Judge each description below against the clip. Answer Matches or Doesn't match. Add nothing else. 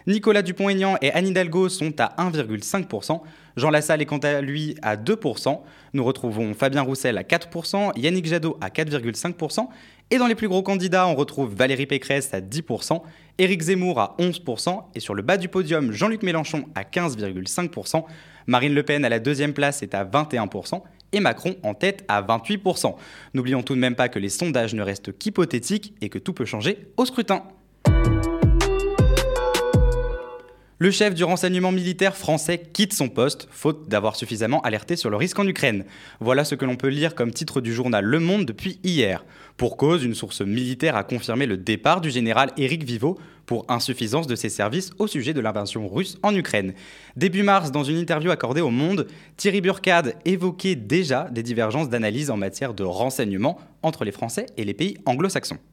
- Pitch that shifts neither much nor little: Doesn't match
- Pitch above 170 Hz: Doesn't match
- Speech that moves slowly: Doesn't match